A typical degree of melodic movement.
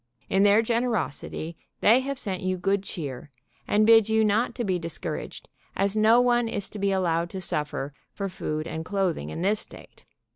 Yes: average, 4.6 semitones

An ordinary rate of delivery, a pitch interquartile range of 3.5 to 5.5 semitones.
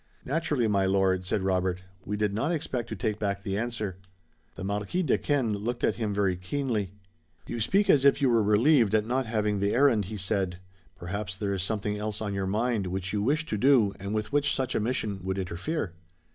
No: fast, 210 wpm; average, 3.8 semitones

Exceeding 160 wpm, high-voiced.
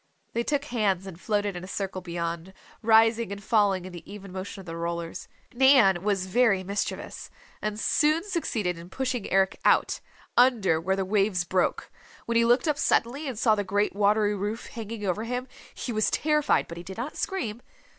Yes: average, 190 wpm; high, 205 Hz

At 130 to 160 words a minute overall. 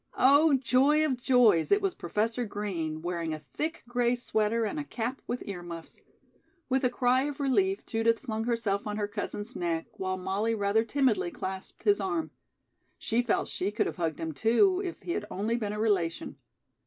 No: average, 190 wpm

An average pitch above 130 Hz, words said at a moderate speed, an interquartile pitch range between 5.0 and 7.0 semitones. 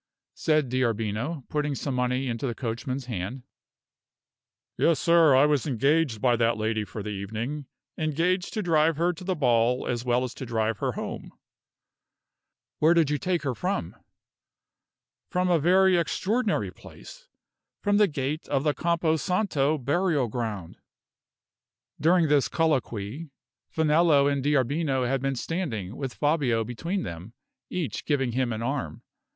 Yes: medium, 140 Hz; average, 145 wpm; average, 5.3 semitones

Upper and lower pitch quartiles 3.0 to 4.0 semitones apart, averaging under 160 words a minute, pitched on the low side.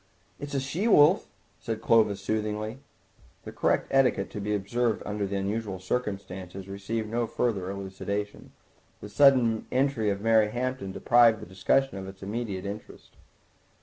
Yes: average, 3.5 semitones; average, 150 wpm; low, 105 Hz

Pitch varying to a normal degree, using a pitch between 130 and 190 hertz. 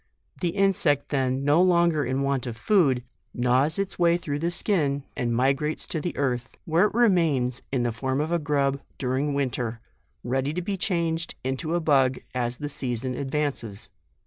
Yes: average, 4.5 semitones; medium, 140 Hz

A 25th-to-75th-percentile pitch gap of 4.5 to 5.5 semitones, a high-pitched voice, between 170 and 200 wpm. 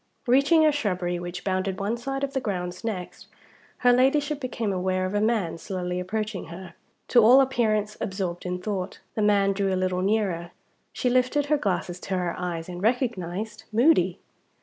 Yes: average, 4.9 semitones; high, 200 Hz; average, 175 wpm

